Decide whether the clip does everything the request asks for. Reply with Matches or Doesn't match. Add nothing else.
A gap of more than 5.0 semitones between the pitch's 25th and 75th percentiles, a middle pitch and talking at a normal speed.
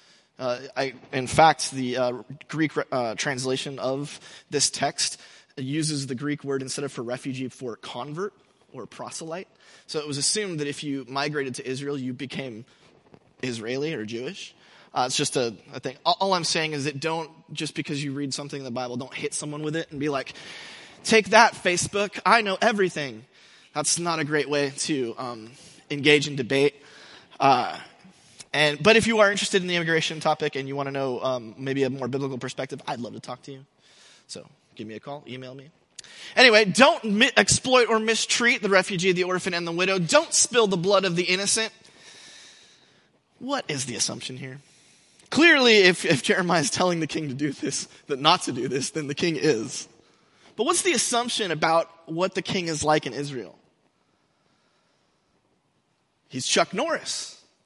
Matches